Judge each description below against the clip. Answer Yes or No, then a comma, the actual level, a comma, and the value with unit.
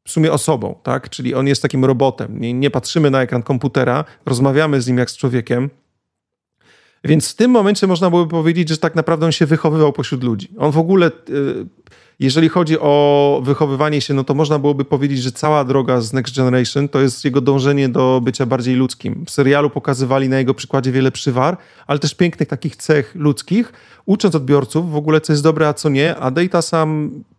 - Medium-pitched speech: Yes, medium, 145 Hz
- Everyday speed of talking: No, fast, 195 wpm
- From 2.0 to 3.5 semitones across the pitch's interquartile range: Yes, average, 3.0 semitones